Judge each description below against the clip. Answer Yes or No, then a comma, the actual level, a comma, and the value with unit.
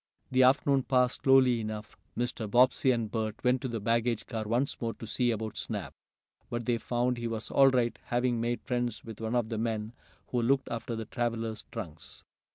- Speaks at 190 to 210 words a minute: Yes, average, 195 wpm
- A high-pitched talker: No, low, 120 Hz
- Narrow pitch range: Yes, narrow, 1.9 semitones